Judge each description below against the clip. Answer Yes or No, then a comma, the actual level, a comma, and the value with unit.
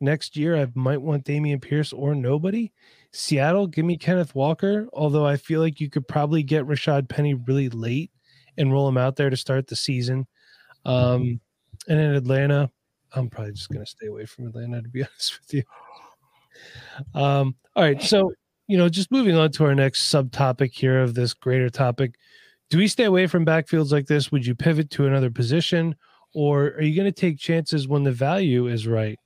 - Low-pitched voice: No, medium, 145 Hz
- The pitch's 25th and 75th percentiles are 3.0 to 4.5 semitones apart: Yes, average, 3.3 semitones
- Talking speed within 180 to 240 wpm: Yes, average, 200 wpm